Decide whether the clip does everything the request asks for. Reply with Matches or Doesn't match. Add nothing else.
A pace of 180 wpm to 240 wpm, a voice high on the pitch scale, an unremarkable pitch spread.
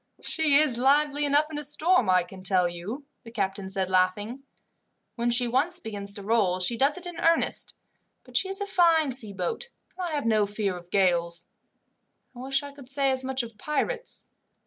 Doesn't match